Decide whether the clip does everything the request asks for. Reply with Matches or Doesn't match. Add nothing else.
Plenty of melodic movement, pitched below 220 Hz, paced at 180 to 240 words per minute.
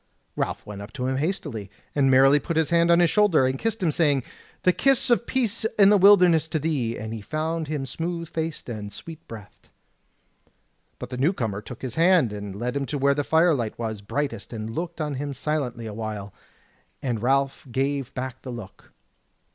Matches